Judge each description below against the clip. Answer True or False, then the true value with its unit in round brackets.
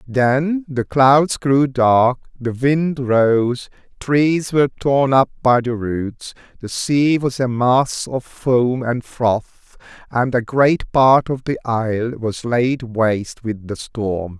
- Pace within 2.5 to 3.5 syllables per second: True (3.1 syllables/s)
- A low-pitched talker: True (125 Hz)